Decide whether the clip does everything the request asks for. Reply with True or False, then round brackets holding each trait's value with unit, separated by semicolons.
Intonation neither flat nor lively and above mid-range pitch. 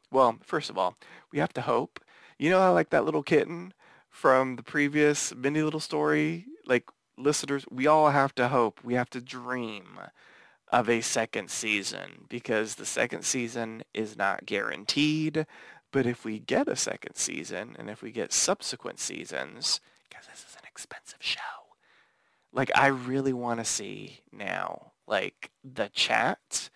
False (3.9 semitones; 135 Hz)